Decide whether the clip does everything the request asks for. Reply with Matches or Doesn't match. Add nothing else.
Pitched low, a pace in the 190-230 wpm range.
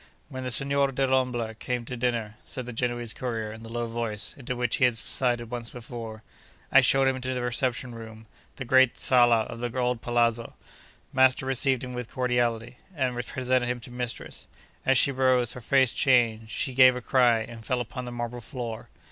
Matches